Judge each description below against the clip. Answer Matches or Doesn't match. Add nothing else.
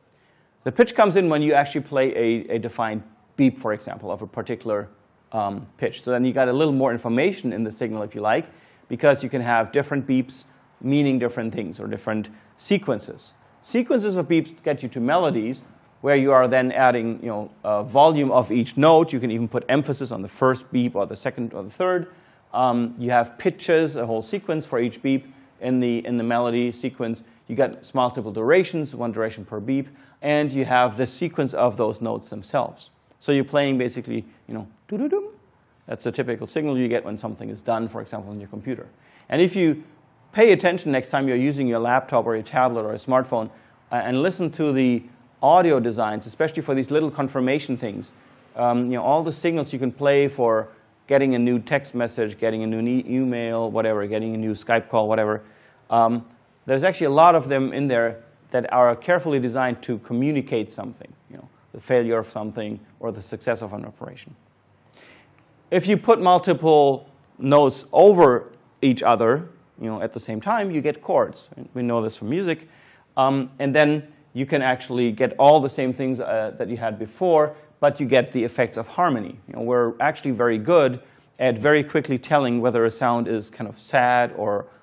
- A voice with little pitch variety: Doesn't match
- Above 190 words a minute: Matches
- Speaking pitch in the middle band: Doesn't match